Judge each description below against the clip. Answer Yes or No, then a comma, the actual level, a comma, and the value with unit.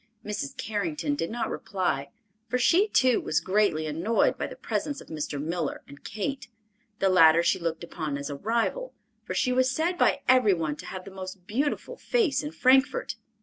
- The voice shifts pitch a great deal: Yes, wide, 7.9 semitones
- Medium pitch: No, high, 200 Hz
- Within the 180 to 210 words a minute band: Yes, average, 190 wpm